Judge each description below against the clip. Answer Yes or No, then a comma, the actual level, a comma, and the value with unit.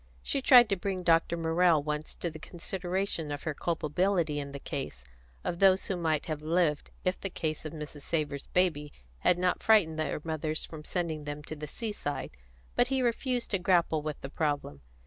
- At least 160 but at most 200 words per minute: Yes, average, 190 wpm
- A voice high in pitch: No, medium, 165 Hz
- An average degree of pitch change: Yes, average, 3.4 semitones